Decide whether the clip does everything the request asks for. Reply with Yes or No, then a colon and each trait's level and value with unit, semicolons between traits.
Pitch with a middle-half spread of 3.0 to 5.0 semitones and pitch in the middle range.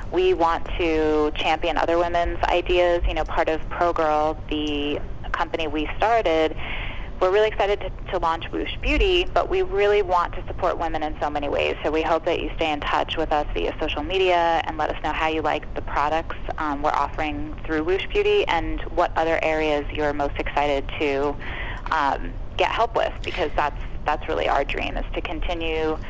No: narrow, 2.5 semitones; medium, 160 Hz